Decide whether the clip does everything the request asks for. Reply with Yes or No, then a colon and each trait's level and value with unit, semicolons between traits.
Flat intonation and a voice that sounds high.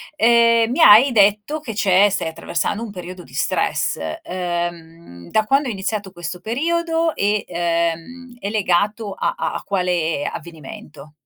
No: average, 5.0 semitones; high, 200 Hz